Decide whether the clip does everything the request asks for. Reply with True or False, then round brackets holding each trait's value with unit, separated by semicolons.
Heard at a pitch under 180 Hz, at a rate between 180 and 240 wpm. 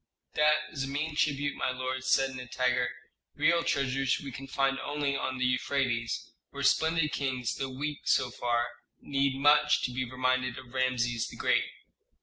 False (135 Hz; 165 wpm)